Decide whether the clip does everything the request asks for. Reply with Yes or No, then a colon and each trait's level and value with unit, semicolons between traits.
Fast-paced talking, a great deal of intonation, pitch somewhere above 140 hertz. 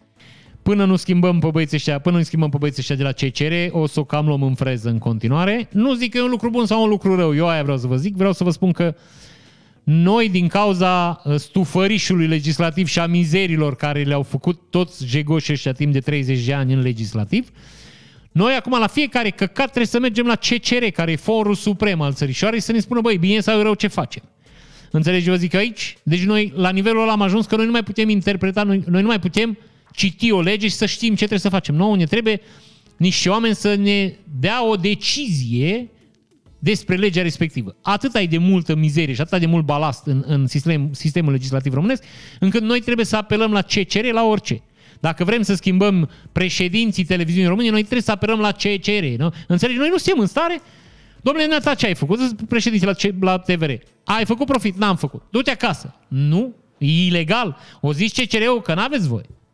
Yes: fast, 210 wpm; wide, 5.9 semitones; medium, 185 Hz